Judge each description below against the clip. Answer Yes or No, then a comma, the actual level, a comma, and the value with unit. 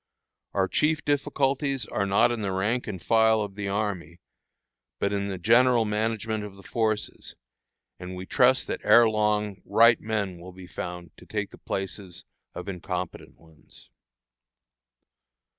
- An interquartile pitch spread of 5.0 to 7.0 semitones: No, average, 3.2 semitones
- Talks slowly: No, average, 150 wpm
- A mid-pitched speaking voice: No, low, 105 Hz